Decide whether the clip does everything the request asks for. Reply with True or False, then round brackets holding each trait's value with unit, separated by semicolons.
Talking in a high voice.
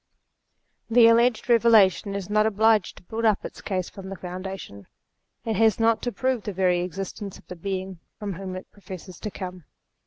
True (195 Hz)